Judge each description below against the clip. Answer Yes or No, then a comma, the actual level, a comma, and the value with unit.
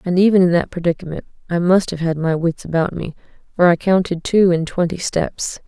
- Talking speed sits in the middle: No, fast, 210 wpm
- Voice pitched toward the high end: No, medium, 175 Hz